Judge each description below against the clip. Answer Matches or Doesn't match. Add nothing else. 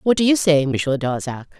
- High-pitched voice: Doesn't match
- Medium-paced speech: Doesn't match